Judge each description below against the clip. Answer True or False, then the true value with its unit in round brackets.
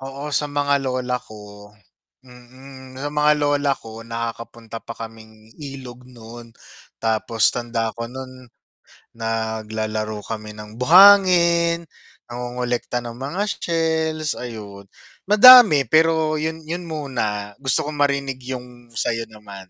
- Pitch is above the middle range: False (125 Hz)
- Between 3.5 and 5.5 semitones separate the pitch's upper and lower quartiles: True (4.5 semitones)